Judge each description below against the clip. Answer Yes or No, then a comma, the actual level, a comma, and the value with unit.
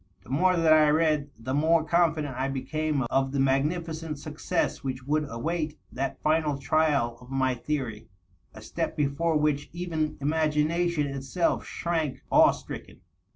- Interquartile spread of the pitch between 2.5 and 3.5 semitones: Yes, average, 2.9 semitones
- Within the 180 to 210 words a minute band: No, average, 155 wpm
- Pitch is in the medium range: Yes, medium, 150 Hz